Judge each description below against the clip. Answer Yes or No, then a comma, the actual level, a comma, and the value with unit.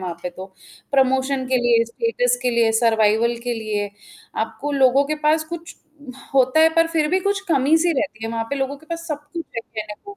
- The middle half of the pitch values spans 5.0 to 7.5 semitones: Yes, wide, 5.4 semitones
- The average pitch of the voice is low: No, very high, 260 Hz